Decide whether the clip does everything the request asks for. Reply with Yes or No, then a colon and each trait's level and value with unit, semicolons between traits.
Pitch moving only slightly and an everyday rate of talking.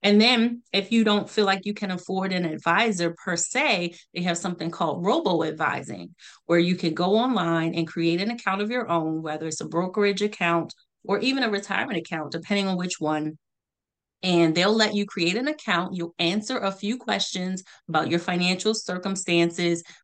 No: average, 3.5 semitones; average, 185 wpm